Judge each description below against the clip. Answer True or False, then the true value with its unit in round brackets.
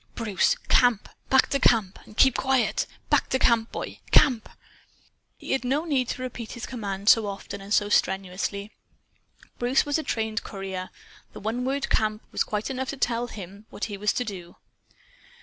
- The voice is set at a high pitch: True (225 Hz)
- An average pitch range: True (4.1 semitones)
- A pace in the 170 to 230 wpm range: True (180 wpm)